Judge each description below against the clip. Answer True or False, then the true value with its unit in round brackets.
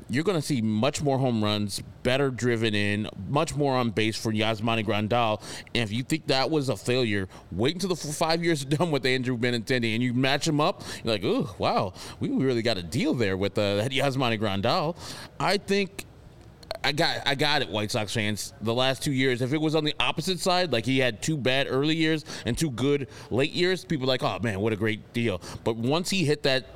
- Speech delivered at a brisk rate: True (230 wpm)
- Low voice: True (130 Hz)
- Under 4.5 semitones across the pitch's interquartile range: False (4.8 semitones)